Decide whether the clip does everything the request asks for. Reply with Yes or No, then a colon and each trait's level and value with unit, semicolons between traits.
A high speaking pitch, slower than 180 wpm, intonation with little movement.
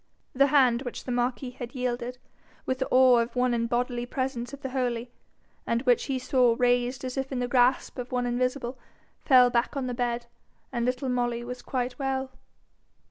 No: very high, 250 Hz; average, 190 wpm; narrow, 1.2 semitones